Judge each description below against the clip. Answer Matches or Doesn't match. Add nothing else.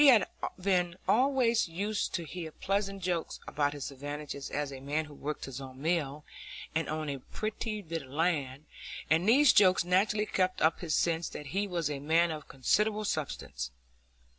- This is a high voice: Doesn't match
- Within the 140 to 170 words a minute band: Doesn't match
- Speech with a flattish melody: Doesn't match